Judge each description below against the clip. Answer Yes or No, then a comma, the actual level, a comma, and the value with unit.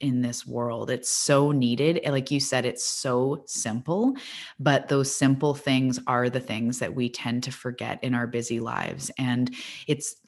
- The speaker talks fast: No, average, 175 wpm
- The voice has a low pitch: Yes, low, 130 Hz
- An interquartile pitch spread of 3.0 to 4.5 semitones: No, narrow, 2.6 semitones